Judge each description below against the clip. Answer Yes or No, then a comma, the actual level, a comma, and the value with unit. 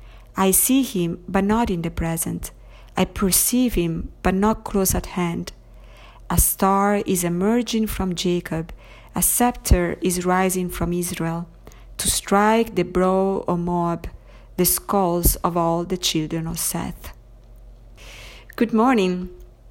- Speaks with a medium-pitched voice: Yes, medium, 180 Hz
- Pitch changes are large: No, average, 2.7 semitones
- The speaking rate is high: No, slow, 135 wpm